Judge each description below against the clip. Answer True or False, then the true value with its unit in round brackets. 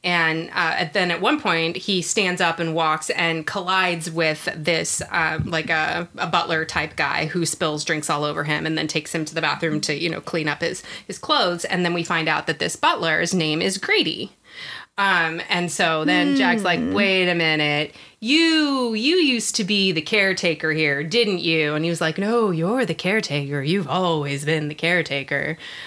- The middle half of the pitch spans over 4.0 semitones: False (3.3 semitones)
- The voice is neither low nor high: True (170 Hz)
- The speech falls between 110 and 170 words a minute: False (200 wpm)